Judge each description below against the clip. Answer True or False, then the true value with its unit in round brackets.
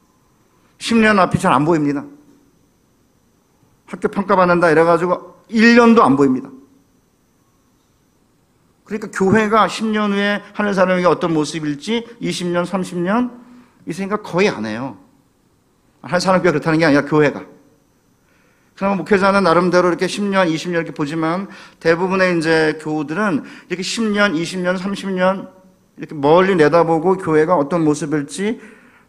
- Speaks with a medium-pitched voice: True (180 Hz)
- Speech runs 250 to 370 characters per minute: True (270 characters per minute)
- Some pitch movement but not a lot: True (4.1 semitones)